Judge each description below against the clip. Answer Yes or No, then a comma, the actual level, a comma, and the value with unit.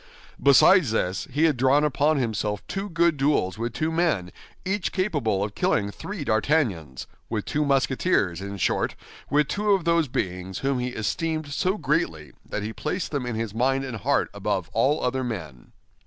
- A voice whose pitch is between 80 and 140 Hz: Yes, low, 135 Hz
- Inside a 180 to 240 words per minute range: No, average, 170 wpm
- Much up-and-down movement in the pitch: Yes, wide, 6.9 semitones